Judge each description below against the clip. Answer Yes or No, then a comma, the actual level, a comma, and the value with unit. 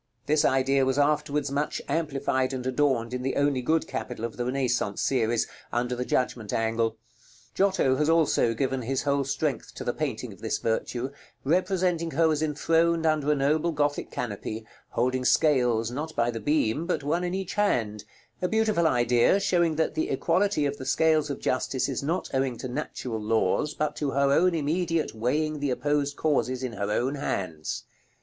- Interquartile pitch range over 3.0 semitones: Yes, average, 4.1 semitones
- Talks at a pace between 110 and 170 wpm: No, average, 180 wpm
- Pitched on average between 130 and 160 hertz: Yes, medium, 140 Hz